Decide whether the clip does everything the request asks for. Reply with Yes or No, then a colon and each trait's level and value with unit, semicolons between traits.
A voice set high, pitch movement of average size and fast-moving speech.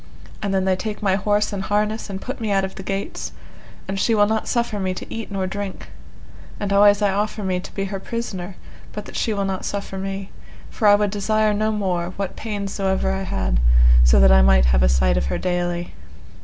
No: high, 195 Hz; narrow, 2.0 semitones; fast, 230 wpm